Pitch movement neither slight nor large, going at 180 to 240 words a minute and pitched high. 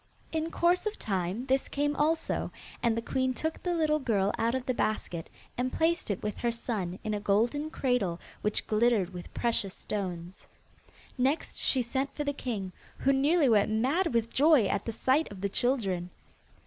No: wide, 5.9 semitones; average, 185 wpm; high, 240 Hz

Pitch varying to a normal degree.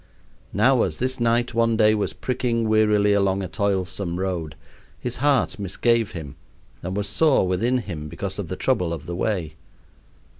Yes: average, 4.1 semitones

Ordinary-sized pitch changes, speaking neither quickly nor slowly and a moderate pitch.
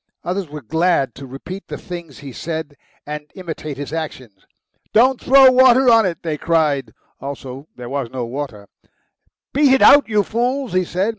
No: wide, 7.5 semitones; average, 170 wpm; medium, 160 Hz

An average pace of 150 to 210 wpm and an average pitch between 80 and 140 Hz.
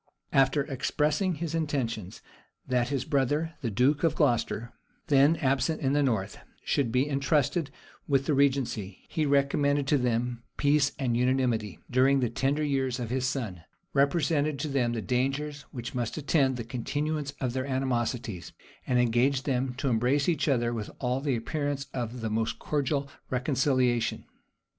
Yes: average, 155 wpm; low, 135 Hz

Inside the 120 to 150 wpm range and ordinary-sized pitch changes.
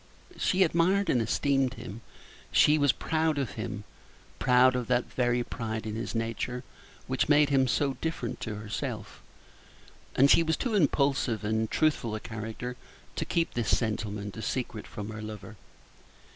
No: average, 160 wpm; average, 4.5 semitones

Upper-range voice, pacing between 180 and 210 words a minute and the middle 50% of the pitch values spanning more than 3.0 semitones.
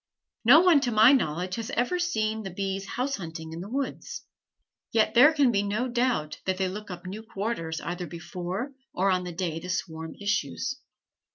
Yes: high, 200 Hz; average, 190 wpm; wide, 5.4 semitones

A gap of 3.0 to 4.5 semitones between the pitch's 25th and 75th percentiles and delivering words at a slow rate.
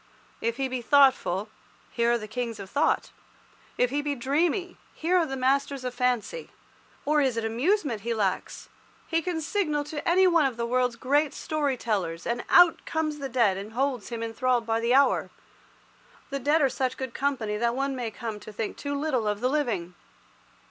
No: average, 4.2 semitones; average, 200 wpm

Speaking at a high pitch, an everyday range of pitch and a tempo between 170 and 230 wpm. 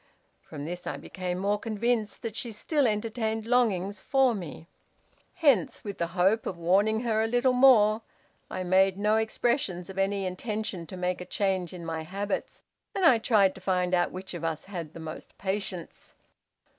Yes: high, 200 Hz; average, 3.6 semitones; average, 180 wpm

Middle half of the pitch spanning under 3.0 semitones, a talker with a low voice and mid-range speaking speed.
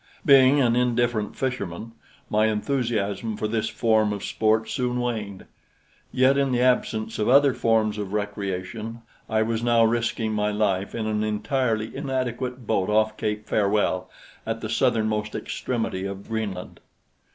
Yes: narrow, 2.4 semitones; low, 110 Hz; average, 145 wpm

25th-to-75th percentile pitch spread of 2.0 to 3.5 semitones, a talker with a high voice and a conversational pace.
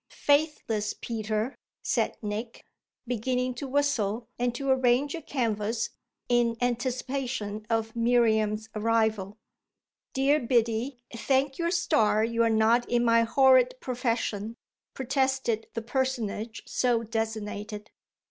No: average, 2.8 semitones; high, 235 Hz; slow, 110 wpm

